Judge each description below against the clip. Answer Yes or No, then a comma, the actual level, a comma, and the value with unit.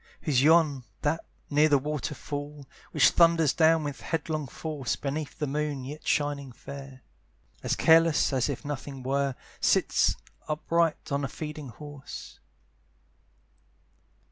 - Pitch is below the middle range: No, medium, 145 Hz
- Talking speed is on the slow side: Yes, slow, 125 wpm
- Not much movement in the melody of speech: Yes, narrow, 2.0 semitones